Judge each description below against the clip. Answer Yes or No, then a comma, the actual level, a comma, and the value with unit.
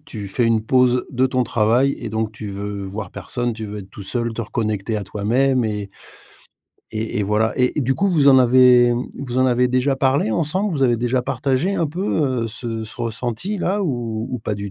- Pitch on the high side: No, low, 120 Hz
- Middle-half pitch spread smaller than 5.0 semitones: Yes, average, 3.2 semitones